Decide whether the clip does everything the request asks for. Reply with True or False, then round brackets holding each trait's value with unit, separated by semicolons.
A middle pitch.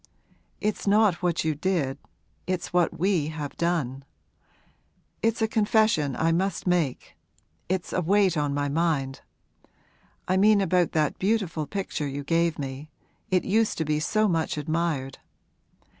True (170 Hz)